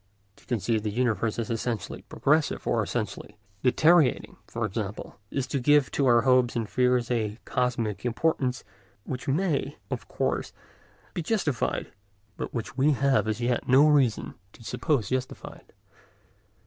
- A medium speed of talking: Yes, average, 145 wpm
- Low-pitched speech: Yes, low, 125 Hz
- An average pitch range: Yes, average, 3.4 semitones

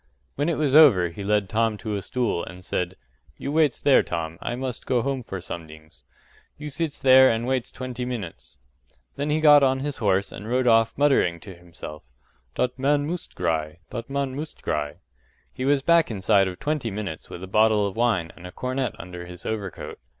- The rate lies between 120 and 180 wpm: No, average, 200 wpm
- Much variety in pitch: Yes, wide, 6.9 semitones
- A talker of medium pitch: No, low, 115 Hz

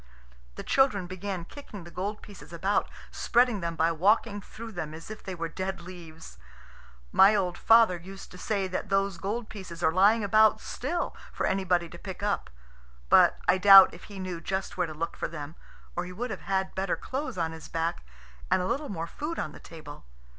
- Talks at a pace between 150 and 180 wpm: No, fast, 205 wpm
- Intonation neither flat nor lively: Yes, average, 3.3 semitones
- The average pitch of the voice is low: No, high, 190 Hz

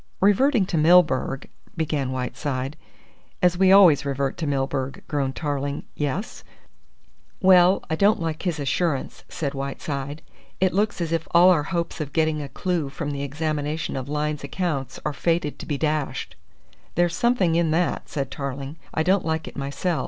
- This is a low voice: No, medium, 155 Hz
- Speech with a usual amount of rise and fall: Yes, average, 3.8 semitones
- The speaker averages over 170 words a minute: No, average, 165 wpm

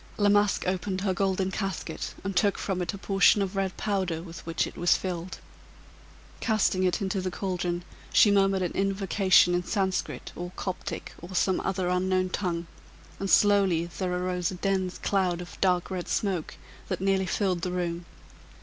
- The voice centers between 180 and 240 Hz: Yes, medium, 185 Hz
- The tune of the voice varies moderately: No, narrow, 1.6 semitones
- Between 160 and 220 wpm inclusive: Yes, average, 175 wpm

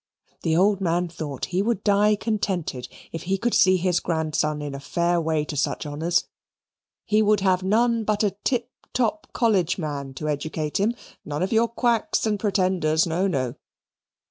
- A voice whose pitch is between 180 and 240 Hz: Yes, medium, 185 Hz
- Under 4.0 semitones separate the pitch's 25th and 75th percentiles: No, average, 5.1 semitones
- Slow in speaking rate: No, average, 175 wpm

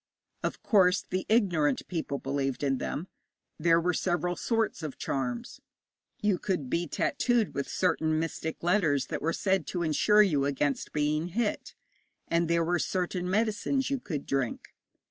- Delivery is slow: No, average, 155 wpm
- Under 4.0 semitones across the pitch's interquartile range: No, average, 4.4 semitones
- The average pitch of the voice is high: No, medium, 170 Hz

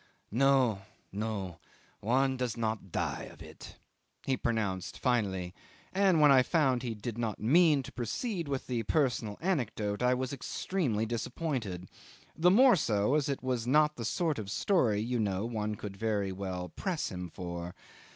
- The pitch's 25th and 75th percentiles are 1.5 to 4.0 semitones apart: No, average, 5.1 semitones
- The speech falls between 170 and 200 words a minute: No, average, 160 wpm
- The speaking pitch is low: Yes, low, 120 Hz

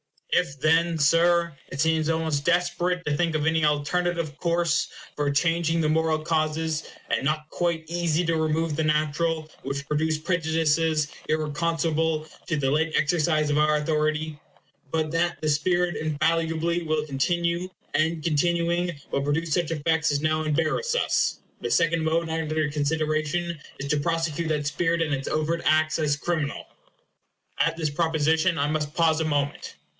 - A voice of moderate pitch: Yes, medium, 160 Hz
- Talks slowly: No, average, 155 wpm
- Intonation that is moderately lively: No, narrow, 1.6 semitones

